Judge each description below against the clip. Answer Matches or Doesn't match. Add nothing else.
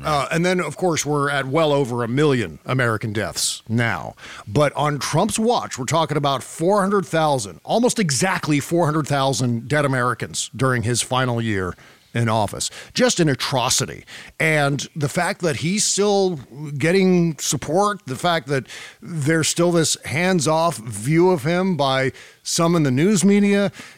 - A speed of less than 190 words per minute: Matches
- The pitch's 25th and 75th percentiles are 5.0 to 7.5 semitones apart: Matches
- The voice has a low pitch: Doesn't match